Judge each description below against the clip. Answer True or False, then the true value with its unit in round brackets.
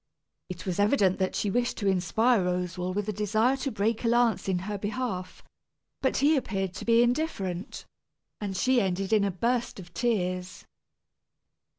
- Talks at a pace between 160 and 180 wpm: True (170 wpm)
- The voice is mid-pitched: False (205 Hz)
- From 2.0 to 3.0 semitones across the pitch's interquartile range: False (4.4 semitones)